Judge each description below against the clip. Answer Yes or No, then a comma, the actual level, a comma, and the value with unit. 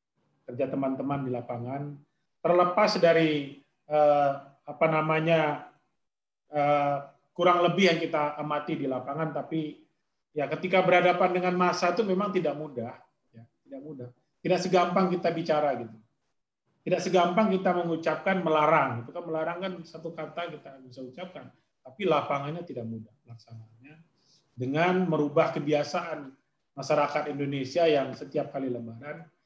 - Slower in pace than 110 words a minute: No, average, 125 wpm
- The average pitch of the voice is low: No, medium, 155 Hz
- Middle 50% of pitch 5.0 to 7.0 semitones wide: No, average, 3.8 semitones